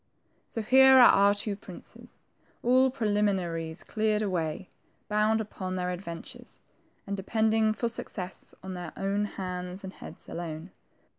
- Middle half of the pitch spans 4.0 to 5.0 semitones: No, average, 3.3 semitones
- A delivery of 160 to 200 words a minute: No, slow, 135 wpm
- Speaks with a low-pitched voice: No, high, 200 Hz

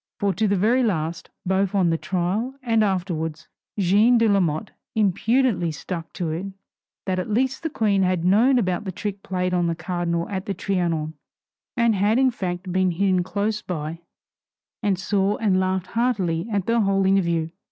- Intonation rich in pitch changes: No, average, 3.2 semitones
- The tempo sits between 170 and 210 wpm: Yes, average, 175 wpm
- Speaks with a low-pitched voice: No, high, 190 Hz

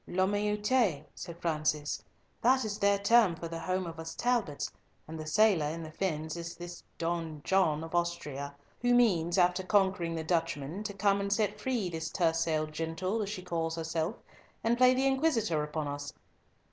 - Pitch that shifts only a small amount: No, average, 4.2 semitones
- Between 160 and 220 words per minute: Yes, average, 180 wpm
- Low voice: No, medium, 175 Hz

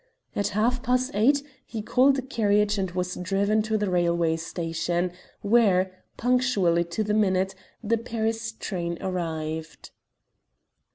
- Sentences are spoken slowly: Yes, slow, 130 wpm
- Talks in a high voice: Yes, high, 205 Hz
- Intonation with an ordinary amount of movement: Yes, average, 4.3 semitones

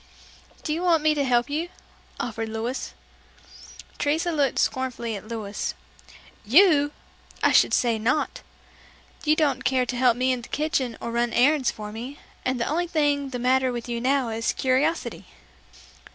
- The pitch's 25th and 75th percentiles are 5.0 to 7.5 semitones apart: No, average, 3.8 semitones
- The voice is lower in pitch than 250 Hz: No, very high, 260 Hz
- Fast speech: No, average, 165 wpm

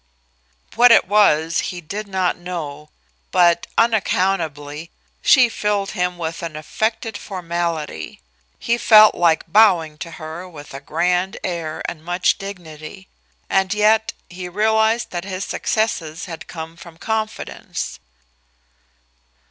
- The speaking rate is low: Yes, slow, 125 wpm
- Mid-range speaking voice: Yes, medium, 180 Hz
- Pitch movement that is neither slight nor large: Yes, average, 4.4 semitones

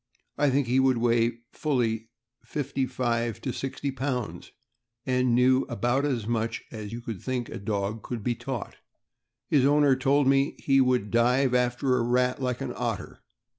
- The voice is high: No, low, 125 Hz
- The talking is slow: No, average, 170 wpm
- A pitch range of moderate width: No, narrow, 2.3 semitones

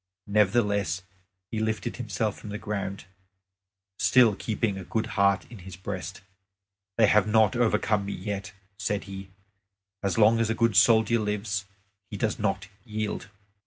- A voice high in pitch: No, low, 105 Hz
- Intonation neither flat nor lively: No, narrow, 2.0 semitones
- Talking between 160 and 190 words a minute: No, average, 150 wpm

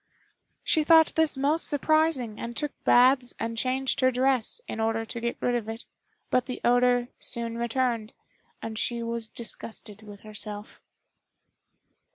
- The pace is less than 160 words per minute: Yes, average, 150 wpm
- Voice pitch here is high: Yes, high, 240 Hz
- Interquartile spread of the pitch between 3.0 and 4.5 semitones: No, narrow, 2.6 semitones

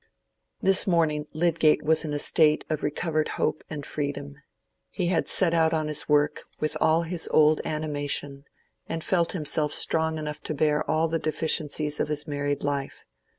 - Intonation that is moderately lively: No, narrow, 1.5 semitones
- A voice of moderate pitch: Yes, medium, 155 Hz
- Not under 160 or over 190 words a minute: Yes, average, 170 wpm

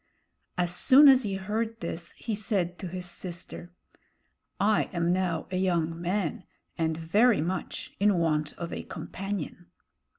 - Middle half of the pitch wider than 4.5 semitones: No, average, 3.2 semitones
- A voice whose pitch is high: No, medium, 180 Hz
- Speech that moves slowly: No, average, 145 wpm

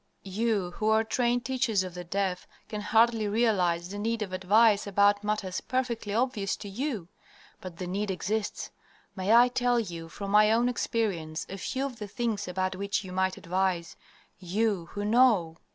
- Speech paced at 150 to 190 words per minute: Yes, average, 175 wpm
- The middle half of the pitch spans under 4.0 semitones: Yes, average, 3.5 semitones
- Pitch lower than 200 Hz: No, high, 205 Hz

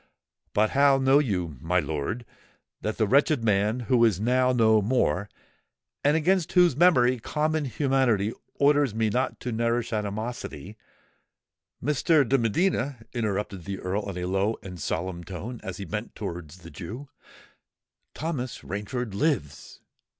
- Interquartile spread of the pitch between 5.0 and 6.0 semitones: Yes, average, 5.3 semitones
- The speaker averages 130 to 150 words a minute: Yes, average, 145 wpm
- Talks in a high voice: No, low, 115 Hz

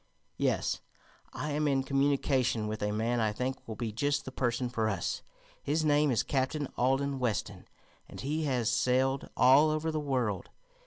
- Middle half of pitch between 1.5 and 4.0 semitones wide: Yes, average, 3.5 semitones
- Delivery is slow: No, average, 170 wpm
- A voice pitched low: Yes, low, 130 Hz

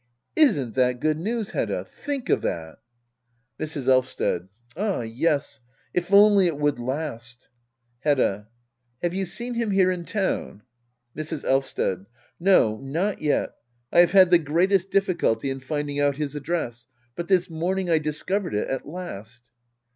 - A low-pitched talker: No, medium, 155 Hz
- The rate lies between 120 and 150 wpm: Yes, average, 145 wpm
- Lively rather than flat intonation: Yes, wide, 6.1 semitones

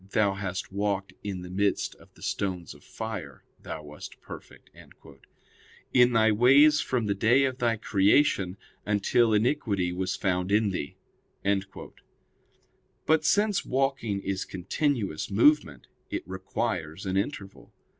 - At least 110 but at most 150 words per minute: Yes, slow, 135 wpm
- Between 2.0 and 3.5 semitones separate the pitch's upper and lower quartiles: No, average, 4.4 semitones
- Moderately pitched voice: No, low, 100 Hz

